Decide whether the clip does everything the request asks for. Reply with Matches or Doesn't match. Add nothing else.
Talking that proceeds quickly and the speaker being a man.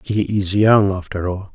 Doesn't match